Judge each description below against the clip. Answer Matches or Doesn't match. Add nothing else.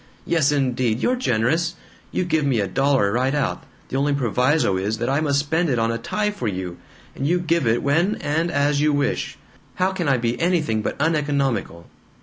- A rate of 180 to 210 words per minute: Matches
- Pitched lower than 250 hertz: Matches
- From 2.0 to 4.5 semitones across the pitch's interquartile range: Doesn't match